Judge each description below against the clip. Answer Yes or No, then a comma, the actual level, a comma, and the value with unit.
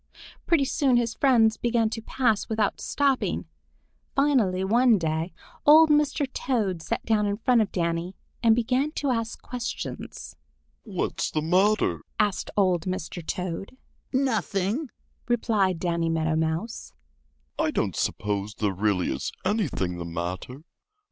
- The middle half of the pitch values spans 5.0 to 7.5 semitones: Yes, wide, 5.5 semitones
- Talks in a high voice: Yes, high, 220 Hz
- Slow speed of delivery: Yes, slow, 110 wpm